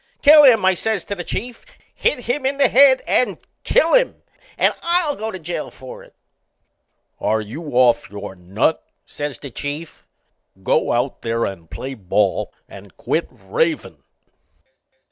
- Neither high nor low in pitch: Yes, medium, 165 Hz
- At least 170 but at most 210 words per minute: No, average, 155 wpm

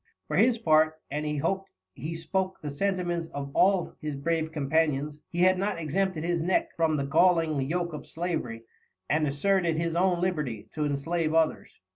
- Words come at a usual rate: Yes, average, 175 wpm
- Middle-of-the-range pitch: Yes, medium, 165 Hz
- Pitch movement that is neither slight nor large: Yes, average, 3.0 semitones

